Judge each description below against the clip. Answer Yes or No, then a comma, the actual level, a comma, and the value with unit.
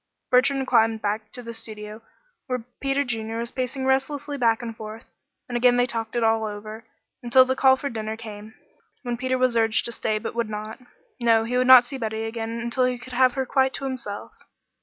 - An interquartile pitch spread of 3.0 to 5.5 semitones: No, narrow, 2.6 semitones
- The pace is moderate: No, fast, 210 wpm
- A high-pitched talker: Yes, high, 235 Hz